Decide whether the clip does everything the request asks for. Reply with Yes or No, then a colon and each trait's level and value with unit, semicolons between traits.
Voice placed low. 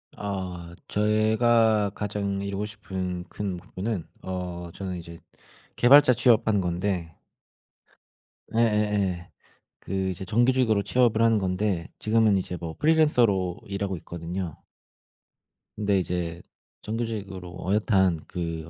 Yes: low, 100 Hz